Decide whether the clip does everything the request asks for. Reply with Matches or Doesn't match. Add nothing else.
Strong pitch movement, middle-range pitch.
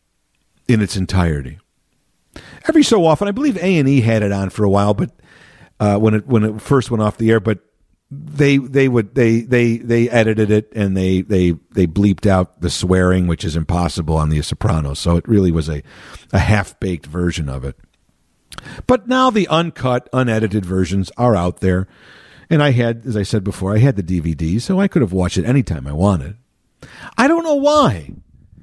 Doesn't match